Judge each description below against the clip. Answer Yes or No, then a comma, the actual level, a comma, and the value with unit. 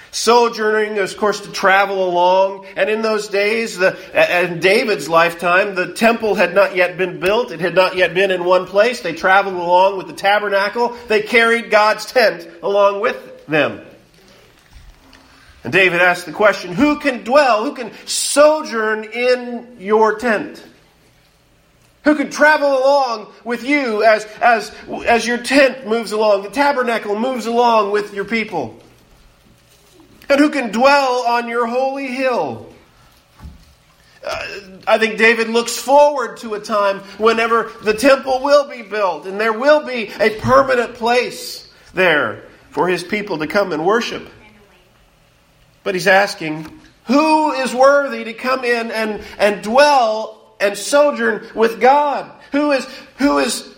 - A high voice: Yes, high, 225 Hz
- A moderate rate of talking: Yes, average, 150 wpm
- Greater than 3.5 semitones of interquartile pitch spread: Yes, average, 4.3 semitones